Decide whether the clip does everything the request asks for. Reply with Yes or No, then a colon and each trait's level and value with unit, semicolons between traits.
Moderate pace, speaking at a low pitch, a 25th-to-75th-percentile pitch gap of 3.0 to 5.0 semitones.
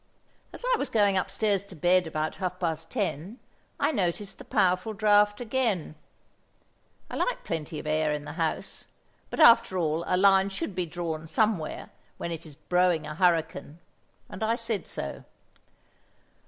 No: average, 160 wpm; medium, 180 Hz; average, 4.4 semitones